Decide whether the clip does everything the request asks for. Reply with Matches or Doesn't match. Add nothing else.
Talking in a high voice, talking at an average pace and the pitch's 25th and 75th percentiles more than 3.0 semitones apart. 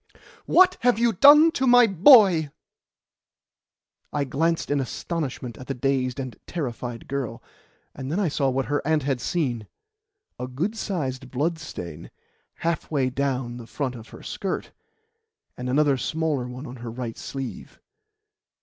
Doesn't match